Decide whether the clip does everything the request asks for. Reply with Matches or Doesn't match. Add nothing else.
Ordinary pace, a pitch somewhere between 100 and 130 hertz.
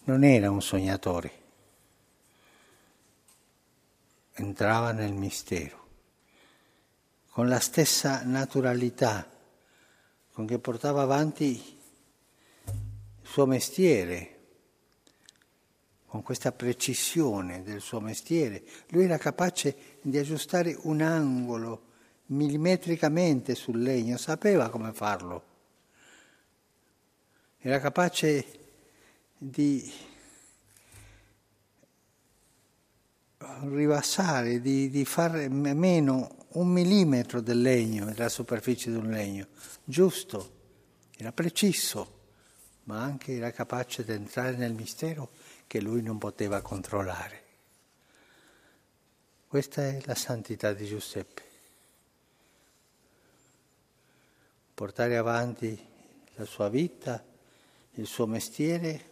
Doesn't match